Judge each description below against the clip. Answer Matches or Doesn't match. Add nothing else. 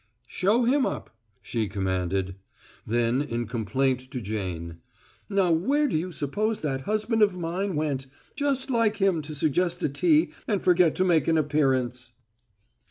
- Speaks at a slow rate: Doesn't match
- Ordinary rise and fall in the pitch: Doesn't match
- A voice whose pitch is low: Doesn't match